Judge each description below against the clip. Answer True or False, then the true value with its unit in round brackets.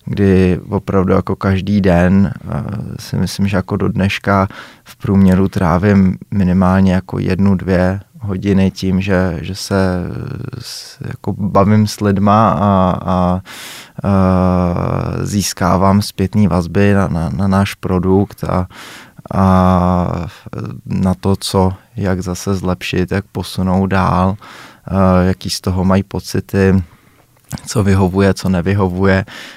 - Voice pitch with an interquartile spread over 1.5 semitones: False (1.2 semitones)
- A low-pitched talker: True (95 Hz)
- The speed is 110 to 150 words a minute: True (120 wpm)